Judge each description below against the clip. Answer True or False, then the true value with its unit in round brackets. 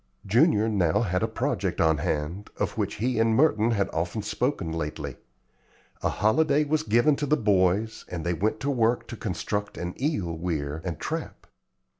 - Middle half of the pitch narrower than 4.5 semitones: False (5.3 semitones)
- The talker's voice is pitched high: False (105 Hz)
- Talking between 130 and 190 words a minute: True (175 wpm)